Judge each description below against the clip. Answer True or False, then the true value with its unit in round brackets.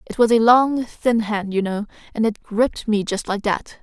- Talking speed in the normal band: False (235 wpm)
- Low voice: False (220 Hz)